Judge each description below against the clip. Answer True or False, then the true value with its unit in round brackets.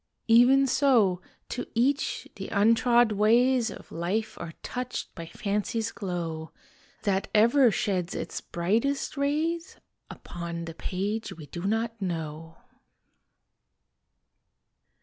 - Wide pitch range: True (5.8 semitones)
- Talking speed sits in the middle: False (110 wpm)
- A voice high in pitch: True (215 Hz)